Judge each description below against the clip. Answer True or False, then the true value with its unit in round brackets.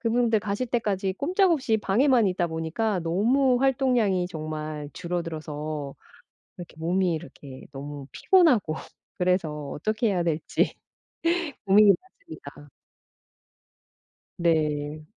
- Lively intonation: True (6.5 semitones)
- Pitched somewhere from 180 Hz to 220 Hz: True (185 Hz)